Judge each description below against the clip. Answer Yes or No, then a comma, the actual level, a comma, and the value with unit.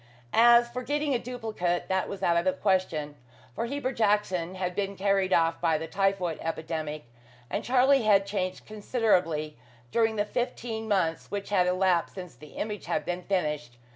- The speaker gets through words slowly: No, average, 170 wpm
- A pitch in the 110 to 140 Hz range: No, high, 195 Hz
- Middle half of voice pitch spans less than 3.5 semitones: No, average, 4.6 semitones